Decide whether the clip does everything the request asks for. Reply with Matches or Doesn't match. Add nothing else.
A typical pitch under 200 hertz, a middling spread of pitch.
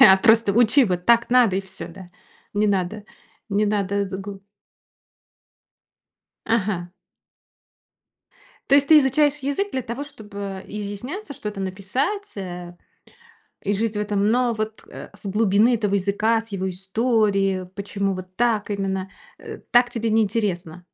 Doesn't match